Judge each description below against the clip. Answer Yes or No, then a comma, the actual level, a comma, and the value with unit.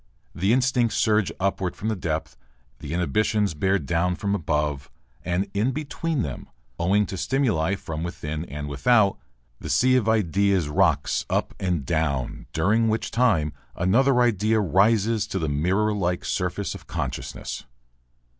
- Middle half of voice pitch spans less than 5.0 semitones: No, average, 5.3 semitones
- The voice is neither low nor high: No, very low, 95 Hz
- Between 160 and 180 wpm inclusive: No, average, 145 wpm